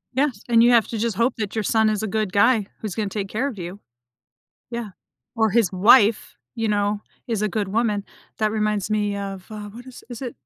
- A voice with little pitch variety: Yes, narrow, 2.2 semitones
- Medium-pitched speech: No, high, 215 Hz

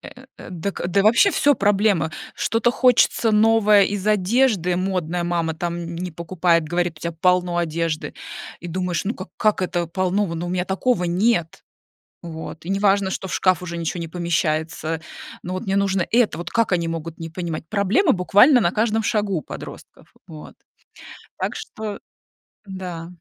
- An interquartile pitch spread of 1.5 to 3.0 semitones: No, average, 3.4 semitones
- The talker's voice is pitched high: No, medium, 180 Hz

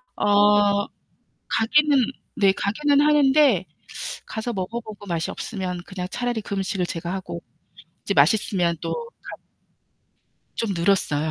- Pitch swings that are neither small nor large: Yes, average, 4.3 semitones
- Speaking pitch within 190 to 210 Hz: Yes, high, 205 Hz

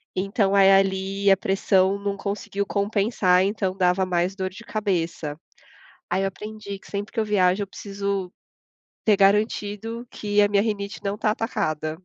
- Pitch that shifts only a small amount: Yes, narrow, 1.5 semitones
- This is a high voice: Yes, high, 200 Hz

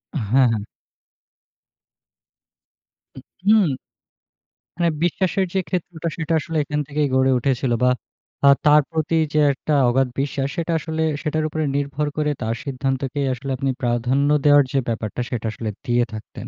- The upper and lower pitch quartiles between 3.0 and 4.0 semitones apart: Yes, average, 3.4 semitones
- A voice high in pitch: No, medium, 140 Hz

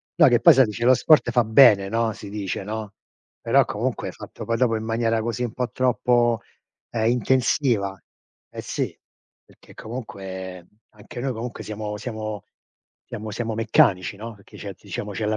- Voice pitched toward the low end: Yes, low, 110 Hz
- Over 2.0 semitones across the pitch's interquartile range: Yes, narrow, 2.6 semitones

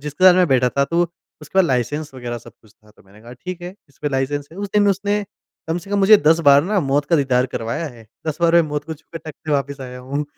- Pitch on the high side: No, medium, 145 Hz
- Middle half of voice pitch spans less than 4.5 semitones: No, average, 4.8 semitones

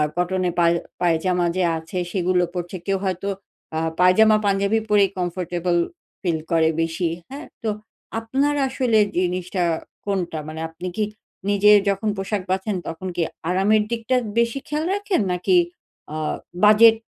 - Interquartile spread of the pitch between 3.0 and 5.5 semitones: Yes, average, 3.5 semitones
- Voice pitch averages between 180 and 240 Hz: Yes, high, 190 Hz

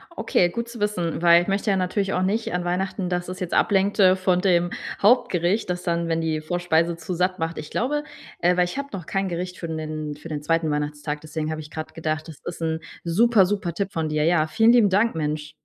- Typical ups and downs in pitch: Yes, average, 3.2 semitones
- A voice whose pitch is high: No, medium, 175 Hz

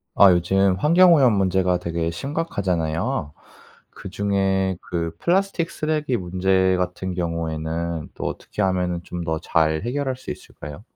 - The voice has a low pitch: Yes, very low, 95 Hz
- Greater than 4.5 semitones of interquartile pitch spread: No, average, 4.0 semitones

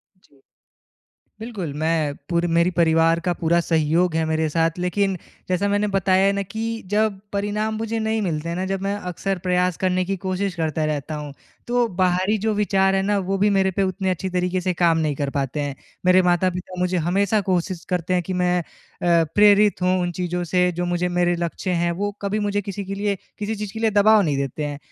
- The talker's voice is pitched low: No, medium, 185 Hz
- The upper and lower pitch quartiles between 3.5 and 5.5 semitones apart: No, average, 2.9 semitones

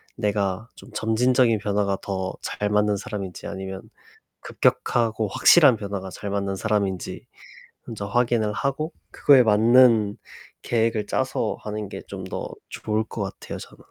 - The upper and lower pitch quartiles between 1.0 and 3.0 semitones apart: Yes, narrow, 2.5 semitones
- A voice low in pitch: Yes, low, 105 Hz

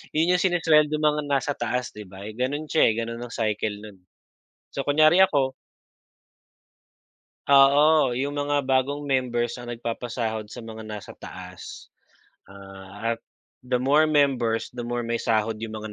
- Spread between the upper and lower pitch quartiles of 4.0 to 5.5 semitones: Yes, average, 4.5 semitones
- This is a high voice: No, low, 120 Hz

